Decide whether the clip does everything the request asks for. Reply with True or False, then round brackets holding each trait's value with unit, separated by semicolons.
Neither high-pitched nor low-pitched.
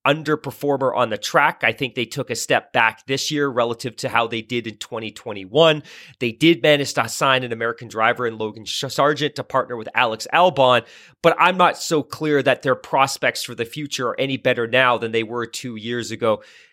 False (125 Hz)